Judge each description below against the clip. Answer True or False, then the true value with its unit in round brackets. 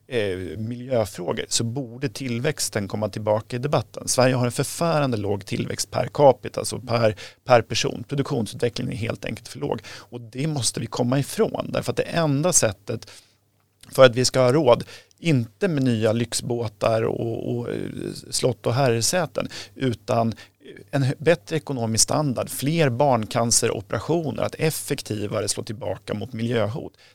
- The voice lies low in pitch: True (120 Hz)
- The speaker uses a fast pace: False (145 wpm)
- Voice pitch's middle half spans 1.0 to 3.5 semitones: False (3.9 semitones)